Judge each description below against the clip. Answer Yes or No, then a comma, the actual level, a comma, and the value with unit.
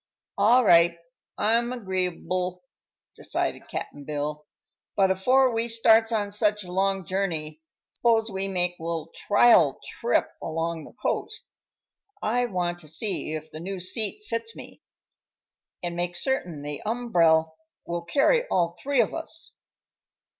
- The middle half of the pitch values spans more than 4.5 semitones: Yes, average, 5.1 semitones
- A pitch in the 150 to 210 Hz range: Yes, high, 190 Hz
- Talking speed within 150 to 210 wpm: No, average, 140 wpm